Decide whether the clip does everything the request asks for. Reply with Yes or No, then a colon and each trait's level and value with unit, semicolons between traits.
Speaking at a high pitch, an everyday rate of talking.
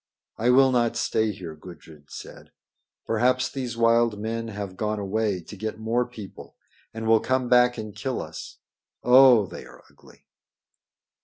No: low, 110 Hz; average, 155 wpm